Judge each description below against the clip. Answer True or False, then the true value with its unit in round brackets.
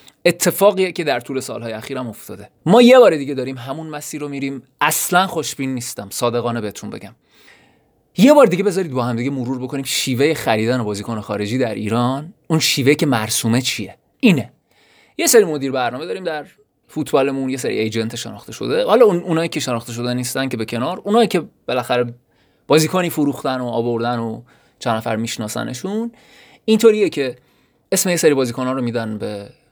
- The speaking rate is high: True (170 wpm)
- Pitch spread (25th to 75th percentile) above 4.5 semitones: True (5.2 semitones)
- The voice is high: False (130 Hz)